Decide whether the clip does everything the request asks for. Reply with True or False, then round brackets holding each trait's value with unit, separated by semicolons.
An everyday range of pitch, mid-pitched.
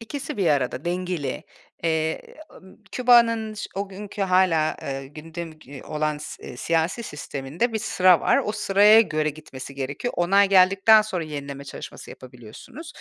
False (5.7 semitones; 175 Hz)